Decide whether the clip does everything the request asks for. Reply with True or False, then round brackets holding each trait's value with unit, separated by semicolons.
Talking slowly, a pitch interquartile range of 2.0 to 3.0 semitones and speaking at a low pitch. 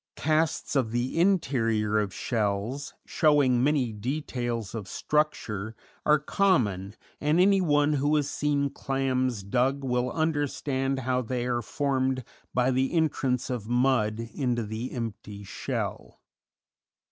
False (125 wpm; 4.1 semitones; 130 Hz)